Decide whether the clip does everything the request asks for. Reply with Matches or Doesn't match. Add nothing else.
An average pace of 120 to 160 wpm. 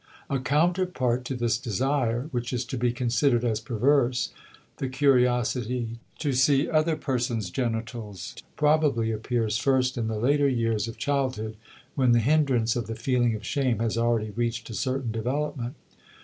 Matches